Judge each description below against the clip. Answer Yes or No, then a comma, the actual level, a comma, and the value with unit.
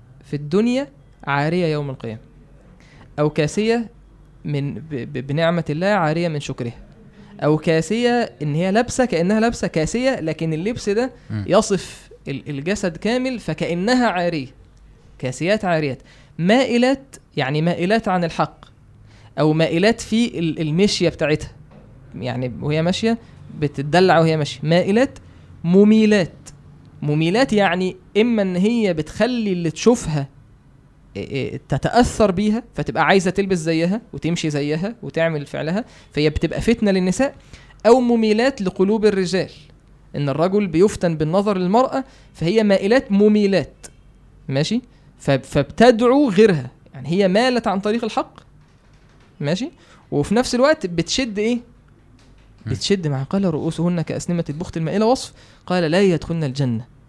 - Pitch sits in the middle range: Yes, medium, 170 Hz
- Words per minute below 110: No, average, 115 wpm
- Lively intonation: Yes, wide, 6.4 semitones